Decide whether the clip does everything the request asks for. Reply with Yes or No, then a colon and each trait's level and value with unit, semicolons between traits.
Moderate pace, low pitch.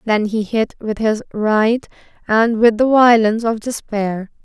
No: average, 160 wpm; high, 220 Hz